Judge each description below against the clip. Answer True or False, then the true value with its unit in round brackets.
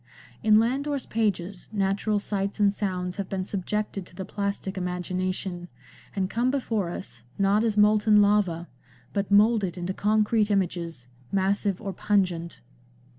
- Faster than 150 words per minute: False (135 wpm)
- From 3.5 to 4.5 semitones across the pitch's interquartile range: False (2.4 semitones)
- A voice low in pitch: False (200 Hz)